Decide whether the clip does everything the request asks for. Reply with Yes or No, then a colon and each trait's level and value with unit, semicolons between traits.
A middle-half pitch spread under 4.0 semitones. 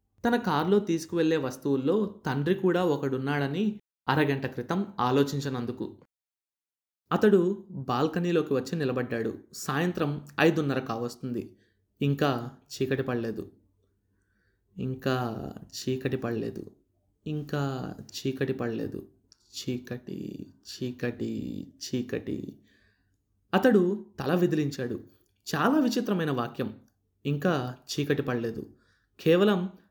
No: wide, 5.4 semitones